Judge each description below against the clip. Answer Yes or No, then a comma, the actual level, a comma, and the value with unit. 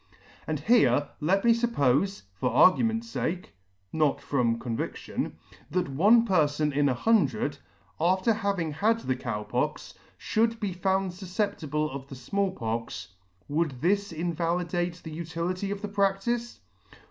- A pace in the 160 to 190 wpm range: No, average, 140 wpm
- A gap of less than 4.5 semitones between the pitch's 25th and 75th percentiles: No, wide, 5.6 semitones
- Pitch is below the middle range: No, medium, 175 Hz